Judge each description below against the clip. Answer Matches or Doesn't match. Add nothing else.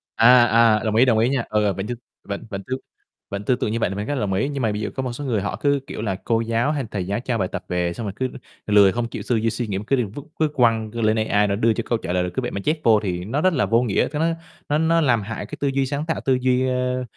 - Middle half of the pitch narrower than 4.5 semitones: Matches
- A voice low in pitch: Matches